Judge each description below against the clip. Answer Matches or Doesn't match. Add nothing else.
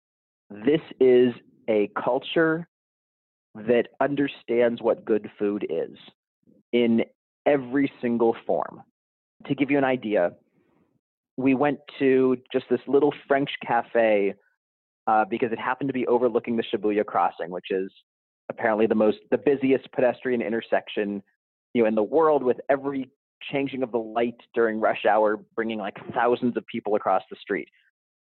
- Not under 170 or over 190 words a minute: Doesn't match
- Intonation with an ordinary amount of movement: Matches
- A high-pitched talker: Doesn't match